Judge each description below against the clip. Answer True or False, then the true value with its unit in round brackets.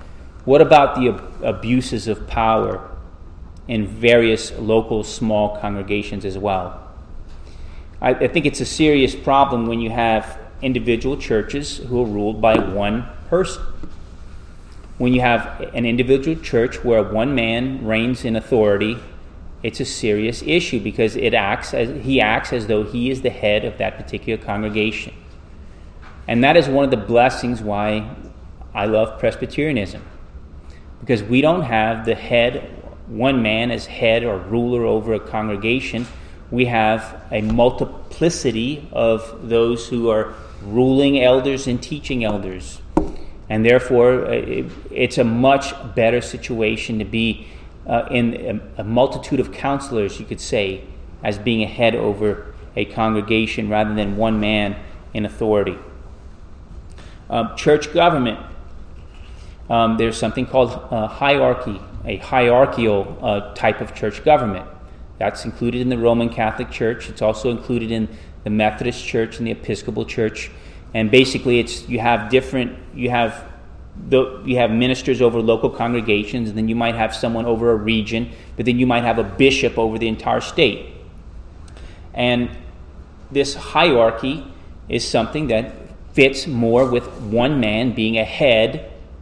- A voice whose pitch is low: True (110 Hz)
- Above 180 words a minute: False (145 wpm)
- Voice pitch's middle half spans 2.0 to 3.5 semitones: True (3.2 semitones)